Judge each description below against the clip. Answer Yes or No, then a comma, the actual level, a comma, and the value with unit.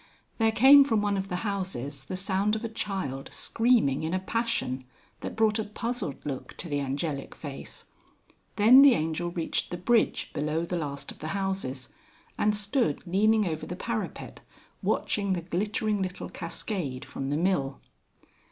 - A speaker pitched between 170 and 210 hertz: Yes, medium, 185 Hz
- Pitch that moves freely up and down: Yes, wide, 6.1 semitones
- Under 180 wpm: Yes, average, 165 wpm